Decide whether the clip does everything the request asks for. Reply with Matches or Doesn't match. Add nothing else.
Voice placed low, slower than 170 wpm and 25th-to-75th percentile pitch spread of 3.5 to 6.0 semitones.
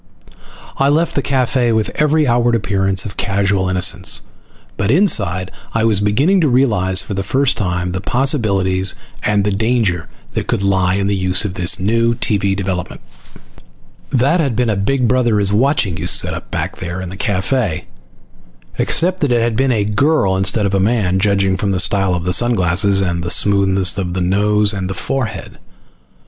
Doesn't match